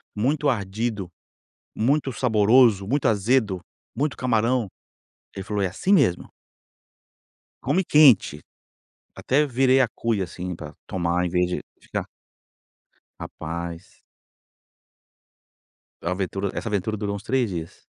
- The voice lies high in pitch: No, low, 105 Hz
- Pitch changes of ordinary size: No, wide, 5.7 semitones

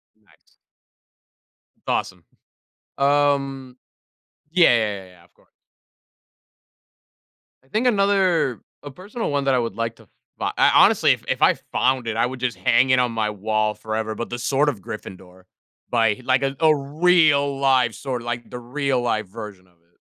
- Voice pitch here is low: Yes, low, 125 Hz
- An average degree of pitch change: Yes, average, 4.4 semitones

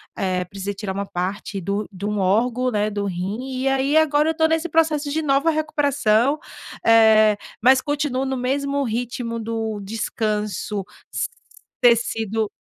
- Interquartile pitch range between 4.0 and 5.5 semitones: Yes, average, 5.1 semitones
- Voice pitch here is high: Yes, high, 230 Hz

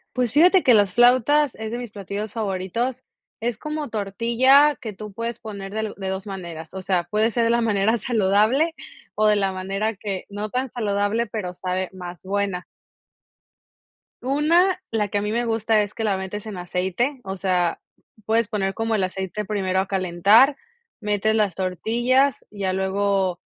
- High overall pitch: Yes, high, 210 Hz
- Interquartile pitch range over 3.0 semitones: Yes, average, 3.5 semitones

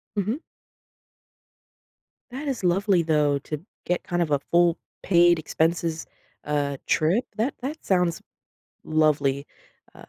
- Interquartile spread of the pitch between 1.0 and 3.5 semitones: No, average, 4.1 semitones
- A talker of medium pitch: Yes, medium, 170 Hz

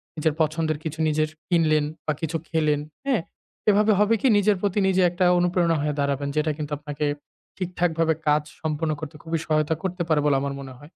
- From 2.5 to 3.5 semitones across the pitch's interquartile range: Yes, average, 2.8 semitones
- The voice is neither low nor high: Yes, medium, 160 Hz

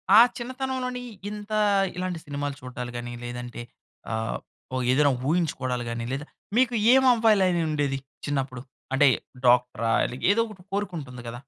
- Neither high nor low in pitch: Yes, medium, 145 Hz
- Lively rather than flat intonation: Yes, wide, 8.6 semitones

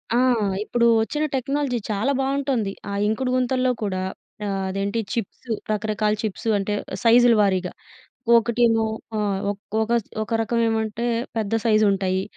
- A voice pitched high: Yes, high, 225 Hz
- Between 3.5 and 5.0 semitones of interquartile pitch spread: No, average, 3.0 semitones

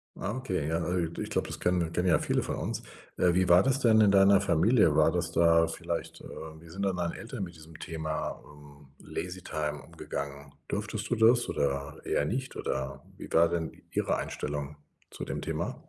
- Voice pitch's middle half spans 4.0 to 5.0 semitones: Yes, average, 4.4 semitones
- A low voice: Yes, very low, 85 Hz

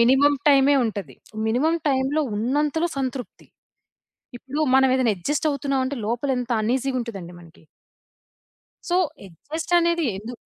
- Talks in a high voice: Yes, very high, 265 Hz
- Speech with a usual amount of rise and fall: Yes, average, 3.7 semitones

